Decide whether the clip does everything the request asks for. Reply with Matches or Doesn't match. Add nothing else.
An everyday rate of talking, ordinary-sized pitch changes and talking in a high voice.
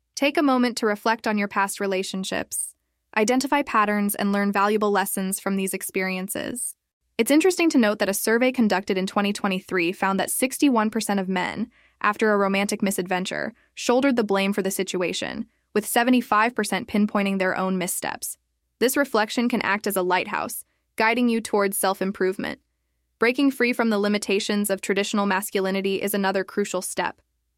Matches